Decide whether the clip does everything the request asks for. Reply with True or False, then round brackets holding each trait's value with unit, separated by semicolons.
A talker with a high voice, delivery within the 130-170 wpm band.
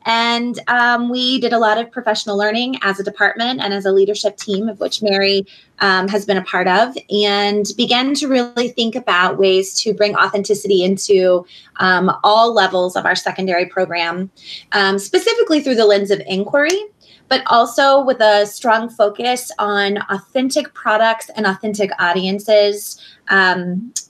True (205 Hz; 160 wpm)